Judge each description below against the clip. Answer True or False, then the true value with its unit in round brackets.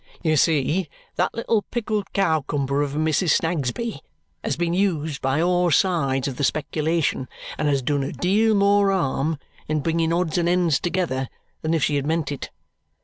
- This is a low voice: False (160 Hz)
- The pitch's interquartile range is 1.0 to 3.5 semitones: False (4.0 semitones)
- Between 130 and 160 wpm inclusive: False (175 wpm)